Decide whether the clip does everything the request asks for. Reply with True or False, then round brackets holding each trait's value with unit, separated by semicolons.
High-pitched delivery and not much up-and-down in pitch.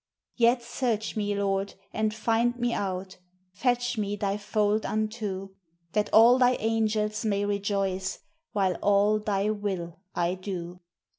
True (210 Hz; 2.0 semitones)